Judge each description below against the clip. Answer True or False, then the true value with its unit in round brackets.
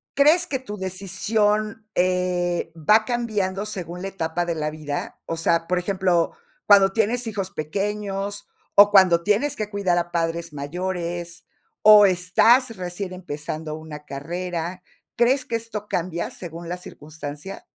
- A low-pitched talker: False (185 Hz)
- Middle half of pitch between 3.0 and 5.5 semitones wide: True (3.6 semitones)